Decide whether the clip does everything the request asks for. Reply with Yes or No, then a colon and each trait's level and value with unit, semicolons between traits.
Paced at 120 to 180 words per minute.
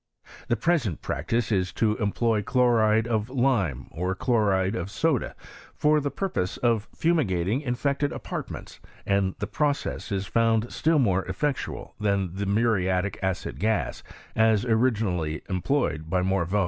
Yes: average, 150 wpm